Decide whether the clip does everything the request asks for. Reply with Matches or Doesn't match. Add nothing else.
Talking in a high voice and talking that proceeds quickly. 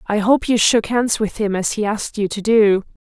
Matches